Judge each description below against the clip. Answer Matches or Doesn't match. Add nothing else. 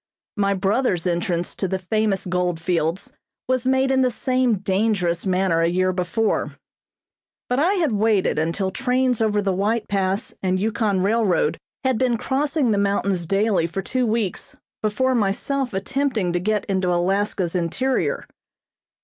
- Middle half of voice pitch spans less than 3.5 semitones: Doesn't match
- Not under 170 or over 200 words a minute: Doesn't match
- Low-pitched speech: Doesn't match